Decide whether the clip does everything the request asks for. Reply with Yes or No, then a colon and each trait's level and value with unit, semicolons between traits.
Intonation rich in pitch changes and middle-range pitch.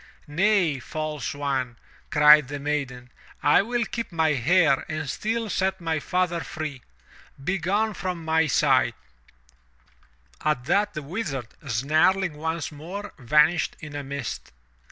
No: average, 4.4 semitones; medium, 155 Hz